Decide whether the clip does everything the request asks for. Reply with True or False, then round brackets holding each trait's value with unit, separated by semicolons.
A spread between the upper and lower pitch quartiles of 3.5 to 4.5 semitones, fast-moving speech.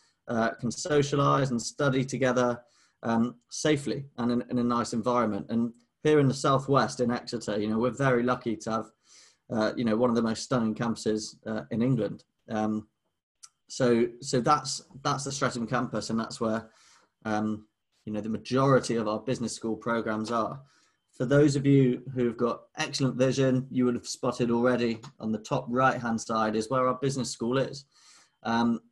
False (2.7 semitones; 185 wpm)